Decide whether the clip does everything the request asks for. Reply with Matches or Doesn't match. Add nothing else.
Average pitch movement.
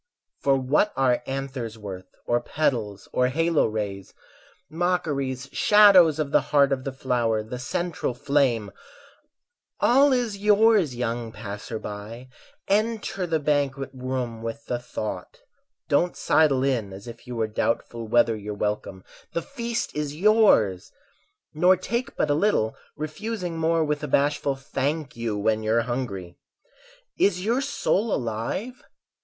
Doesn't match